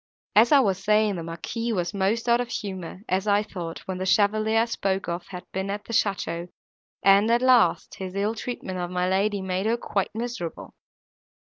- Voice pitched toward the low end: No, high, 200 Hz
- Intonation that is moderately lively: Yes, average, 3.1 semitones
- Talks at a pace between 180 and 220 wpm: Yes, average, 200 wpm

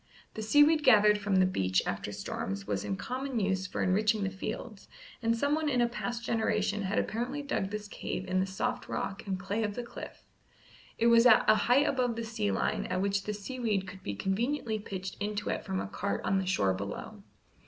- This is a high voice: Yes, high, 210 Hz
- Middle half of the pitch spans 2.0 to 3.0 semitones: No, average, 3.8 semitones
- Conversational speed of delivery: No, fast, 210 wpm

